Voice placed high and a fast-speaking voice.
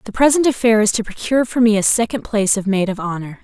Yes: high, 220 Hz; fast, 260 wpm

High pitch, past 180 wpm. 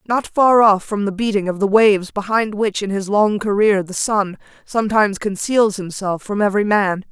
Yes: high, 205 Hz; average, 195 wpm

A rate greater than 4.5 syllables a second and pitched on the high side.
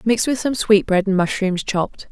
Yes: 5.0 syllables/s; high, 205 Hz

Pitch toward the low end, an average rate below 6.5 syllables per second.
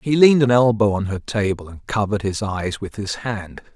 Yes: low, 105 Hz; 5.3 syllables/s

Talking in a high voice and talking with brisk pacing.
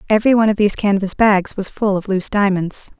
Yes: high, 200 Hz; fast, 220 wpm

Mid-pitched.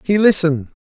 Yes: medium, 170 Hz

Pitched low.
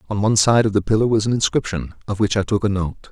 Yes: low, 105 Hz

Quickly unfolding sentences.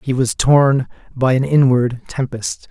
No: average, 155 wpm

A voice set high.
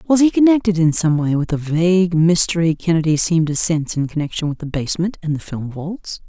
No: medium, 170 Hz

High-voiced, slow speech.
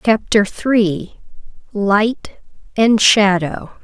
Yes: high, 205 Hz; slow, 65 wpm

